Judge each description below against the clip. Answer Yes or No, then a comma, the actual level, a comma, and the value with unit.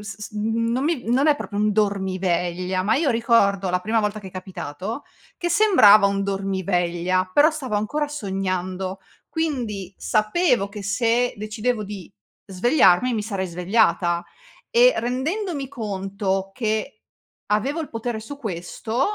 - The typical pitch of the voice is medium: No, high, 210 Hz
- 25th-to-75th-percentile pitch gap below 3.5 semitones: No, average, 4.4 semitones